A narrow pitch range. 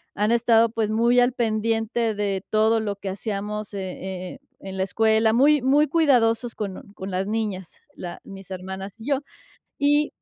No: average, 3.2 semitones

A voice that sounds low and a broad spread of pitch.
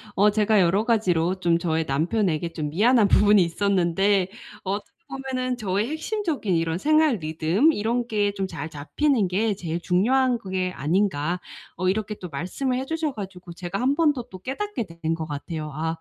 No: high, 195 Hz; wide, 5.9 semitones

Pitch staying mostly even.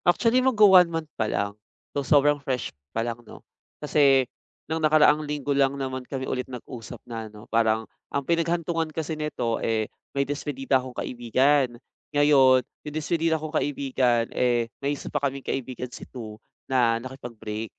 No: average, 3.9 semitones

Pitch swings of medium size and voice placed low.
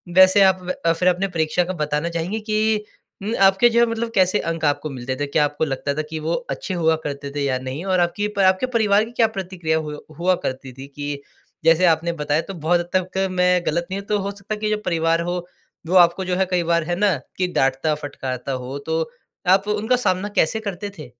No: average, 4.0 semitones; medium, 175 Hz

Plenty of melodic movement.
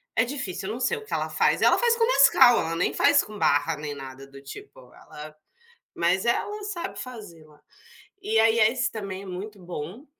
Yes: wide, 8.8 semitones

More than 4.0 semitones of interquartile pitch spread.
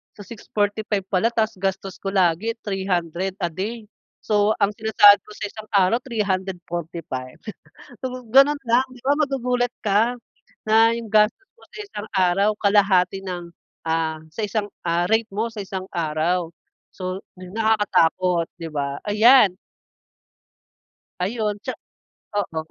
No: average, 3.6 semitones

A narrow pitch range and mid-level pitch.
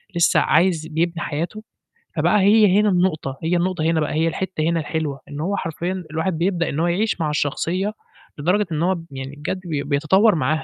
No: average, 3.4 semitones; medium, 165 Hz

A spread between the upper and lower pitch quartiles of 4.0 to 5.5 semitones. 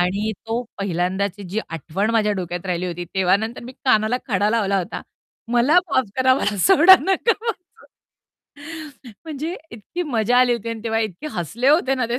Yes: average, 5.1 semitones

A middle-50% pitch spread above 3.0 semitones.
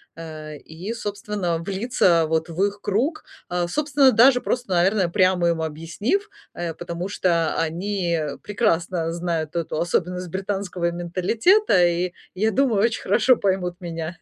Yes: average, 3.6 semitones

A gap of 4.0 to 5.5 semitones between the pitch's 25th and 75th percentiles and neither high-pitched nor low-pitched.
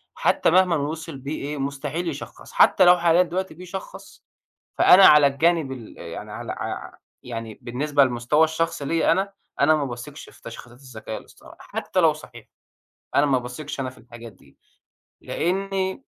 Yes: average, 5.1 semitones; medium, 145 Hz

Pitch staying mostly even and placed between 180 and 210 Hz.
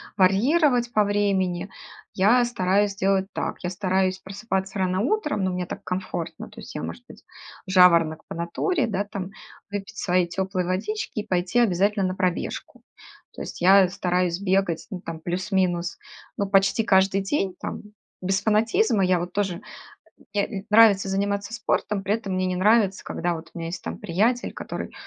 Yes: narrow, 2.1 semitones; high, 190 Hz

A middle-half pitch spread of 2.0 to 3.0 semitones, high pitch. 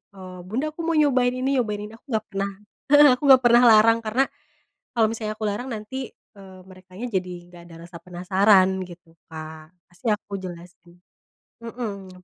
No: average, 4.3 semitones; high, 205 Hz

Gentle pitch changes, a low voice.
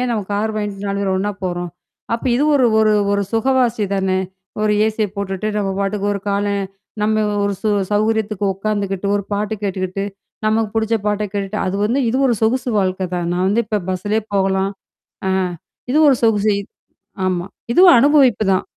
No: narrow, 2.2 semitones; high, 205 Hz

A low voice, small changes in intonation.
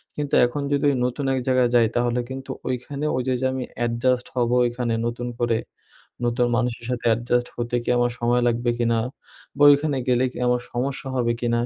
Yes: low, 120 Hz; narrow, 1.4 semitones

